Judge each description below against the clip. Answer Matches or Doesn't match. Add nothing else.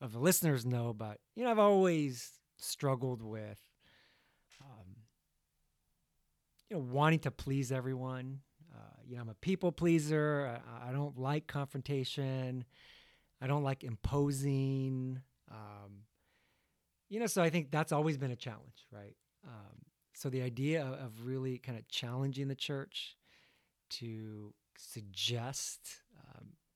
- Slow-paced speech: Matches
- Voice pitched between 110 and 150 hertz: Matches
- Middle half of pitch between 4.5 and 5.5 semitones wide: Doesn't match